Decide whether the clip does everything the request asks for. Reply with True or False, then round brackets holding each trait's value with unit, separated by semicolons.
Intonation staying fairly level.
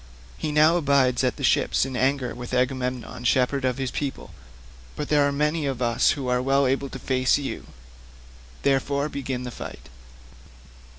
True (1.9 semitones)